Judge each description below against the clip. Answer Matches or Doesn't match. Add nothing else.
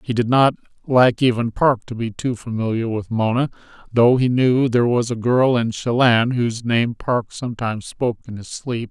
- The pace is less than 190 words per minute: Doesn't match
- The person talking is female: Doesn't match